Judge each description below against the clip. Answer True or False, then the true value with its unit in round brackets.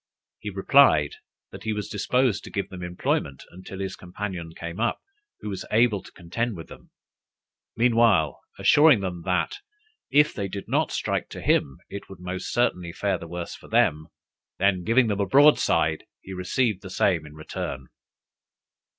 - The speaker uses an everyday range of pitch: True (4.0 semitones)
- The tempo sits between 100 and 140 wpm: False (170 wpm)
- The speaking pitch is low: True (95 Hz)